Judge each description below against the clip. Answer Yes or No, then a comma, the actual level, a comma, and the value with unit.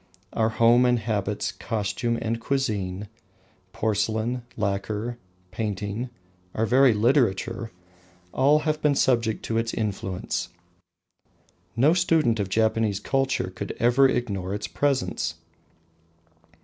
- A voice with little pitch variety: No, average, 3.3 semitones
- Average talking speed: No, slow, 110 wpm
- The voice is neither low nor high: No, low, 115 Hz